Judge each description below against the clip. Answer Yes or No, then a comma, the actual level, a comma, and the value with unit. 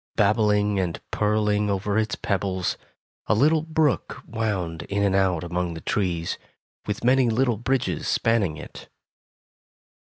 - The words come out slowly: Yes, slow, 130 wpm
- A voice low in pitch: Yes, low, 105 Hz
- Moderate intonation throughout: Yes, average, 3.3 semitones